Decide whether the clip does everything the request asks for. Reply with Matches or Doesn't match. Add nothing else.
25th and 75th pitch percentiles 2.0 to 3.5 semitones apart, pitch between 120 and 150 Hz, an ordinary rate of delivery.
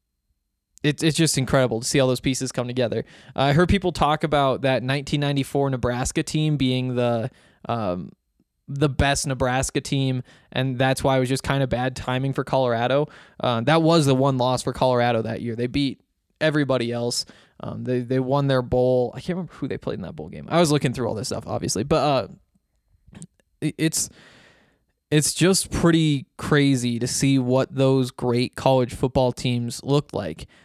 Matches